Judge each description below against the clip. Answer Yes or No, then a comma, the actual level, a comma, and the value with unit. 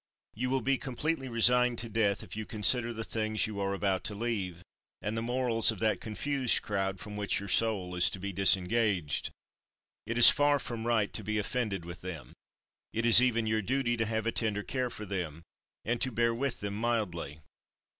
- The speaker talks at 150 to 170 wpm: No, average, 200 wpm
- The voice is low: Yes, low, 110 Hz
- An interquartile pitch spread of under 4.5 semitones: Yes, average, 3.1 semitones